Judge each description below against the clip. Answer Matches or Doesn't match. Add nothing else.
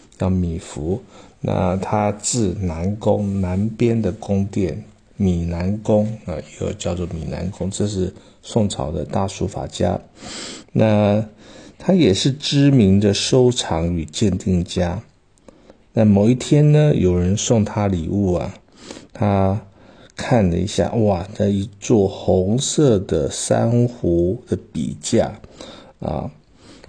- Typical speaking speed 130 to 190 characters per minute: Matches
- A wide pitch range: Doesn't match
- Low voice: Matches